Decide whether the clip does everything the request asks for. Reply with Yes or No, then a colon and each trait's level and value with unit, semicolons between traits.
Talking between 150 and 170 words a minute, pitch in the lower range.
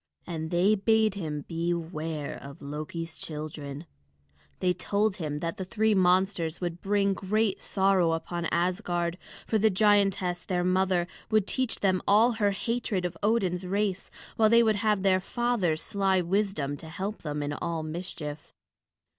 No: average, 155 wpm; medium, 185 Hz